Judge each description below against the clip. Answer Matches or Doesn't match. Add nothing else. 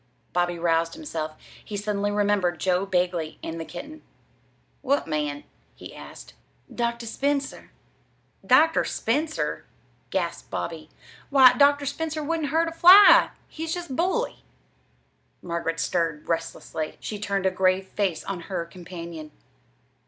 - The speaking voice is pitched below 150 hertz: Doesn't match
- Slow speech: Matches